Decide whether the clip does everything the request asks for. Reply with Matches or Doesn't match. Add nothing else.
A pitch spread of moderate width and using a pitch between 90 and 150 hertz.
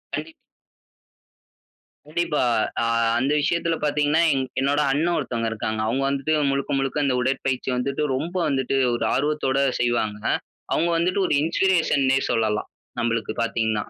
Matches